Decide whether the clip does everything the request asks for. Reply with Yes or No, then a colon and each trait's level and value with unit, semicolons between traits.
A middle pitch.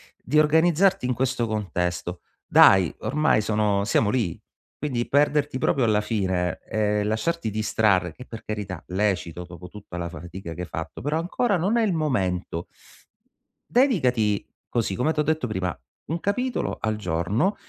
No: low, 110 Hz